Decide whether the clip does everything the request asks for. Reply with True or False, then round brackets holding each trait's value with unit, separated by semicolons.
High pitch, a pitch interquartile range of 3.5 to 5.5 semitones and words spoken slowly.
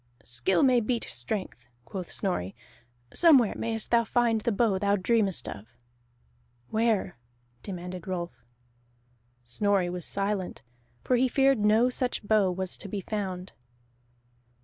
True (200 Hz; 4.0 semitones; 125 wpm)